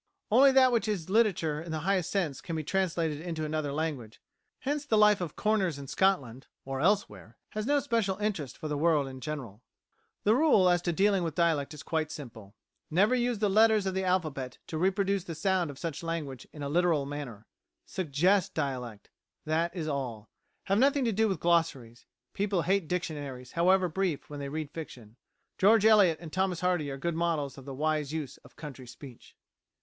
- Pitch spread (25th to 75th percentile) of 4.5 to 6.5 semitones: Yes, average, 5.2 semitones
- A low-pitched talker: No, medium, 165 Hz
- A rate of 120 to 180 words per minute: No, average, 195 wpm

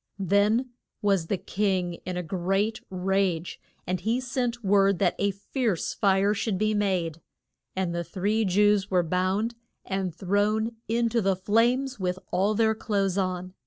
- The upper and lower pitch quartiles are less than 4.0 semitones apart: Yes, average, 2.7 semitones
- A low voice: No, high, 195 Hz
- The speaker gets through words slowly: No, average, 160 wpm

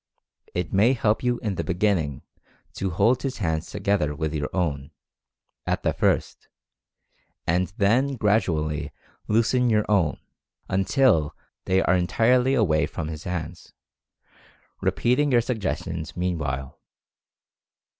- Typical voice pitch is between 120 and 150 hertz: No, very low, 95 Hz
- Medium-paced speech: No, slow, 120 wpm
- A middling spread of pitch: No, wide, 6.3 semitones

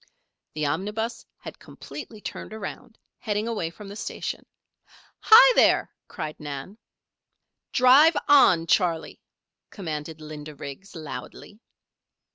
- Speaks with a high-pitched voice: Yes, high, 195 Hz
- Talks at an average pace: No, slow, 105 wpm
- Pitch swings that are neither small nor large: No, wide, 6.5 semitones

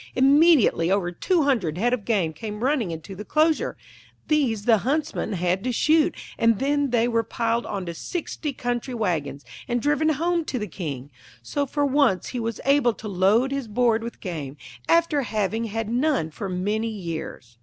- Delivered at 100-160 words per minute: No, average, 180 wpm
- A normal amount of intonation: No, wide, 6.5 semitones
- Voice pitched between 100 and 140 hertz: No, high, 230 Hz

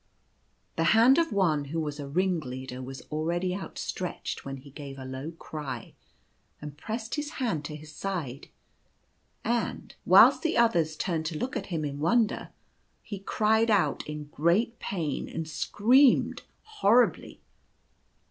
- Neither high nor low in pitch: Yes, medium, 165 Hz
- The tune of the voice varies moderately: No, wide, 6.8 semitones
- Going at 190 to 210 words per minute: No, average, 145 wpm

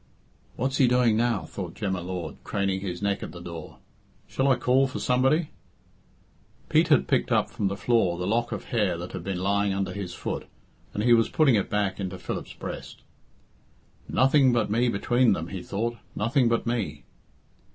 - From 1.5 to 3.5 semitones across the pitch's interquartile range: No, average, 4.3 semitones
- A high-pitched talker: No, low, 105 Hz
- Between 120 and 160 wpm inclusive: No, average, 190 wpm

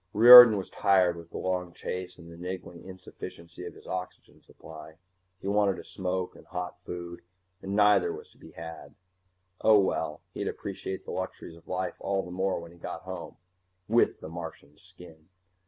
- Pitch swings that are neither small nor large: No, narrow, 2.0 semitones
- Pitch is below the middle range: Yes, very low, 90 Hz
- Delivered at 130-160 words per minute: No, average, 180 wpm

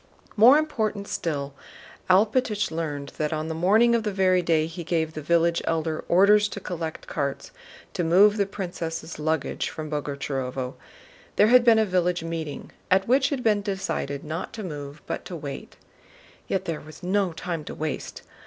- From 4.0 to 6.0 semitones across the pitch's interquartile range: Yes, average, 4.6 semitones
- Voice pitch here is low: No, medium, 170 Hz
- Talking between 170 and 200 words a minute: Yes, average, 175 wpm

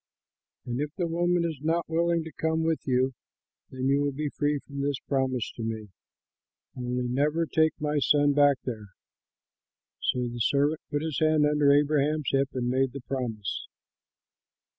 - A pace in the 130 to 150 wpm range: No, average, 165 wpm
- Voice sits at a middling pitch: Yes, medium, 145 Hz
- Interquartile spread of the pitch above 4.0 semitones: No, average, 3.2 semitones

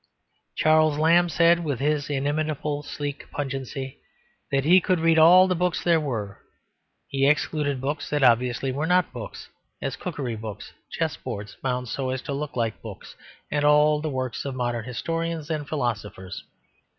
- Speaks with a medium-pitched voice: Yes, medium, 145 Hz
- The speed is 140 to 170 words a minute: Yes, average, 160 wpm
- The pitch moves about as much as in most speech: Yes, average, 3.4 semitones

